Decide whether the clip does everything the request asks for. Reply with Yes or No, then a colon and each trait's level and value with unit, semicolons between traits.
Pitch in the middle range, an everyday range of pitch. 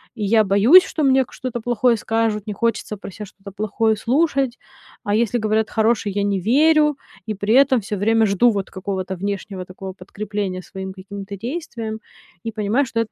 No: high, 215 Hz; average, 3.0 semitones